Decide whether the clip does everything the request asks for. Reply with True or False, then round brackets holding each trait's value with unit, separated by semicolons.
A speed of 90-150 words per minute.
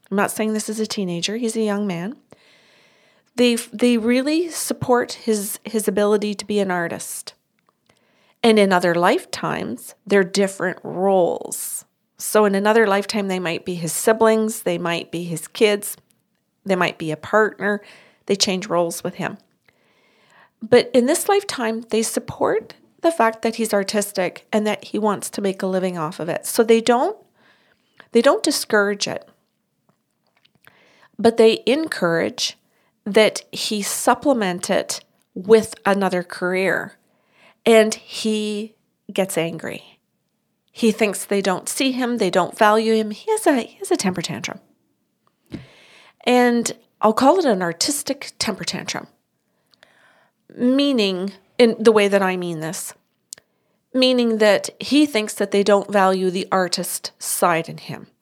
True (145 wpm)